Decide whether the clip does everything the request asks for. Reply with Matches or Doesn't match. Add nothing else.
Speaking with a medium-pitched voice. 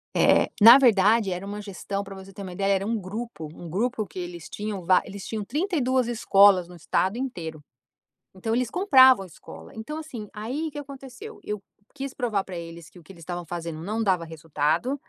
Doesn't match